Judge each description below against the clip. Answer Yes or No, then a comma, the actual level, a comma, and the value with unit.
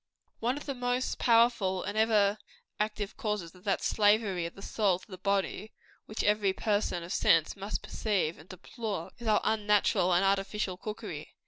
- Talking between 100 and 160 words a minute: No, average, 175 wpm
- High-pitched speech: Yes, high, 205 Hz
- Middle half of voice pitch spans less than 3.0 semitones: Yes, narrow, 2.6 semitones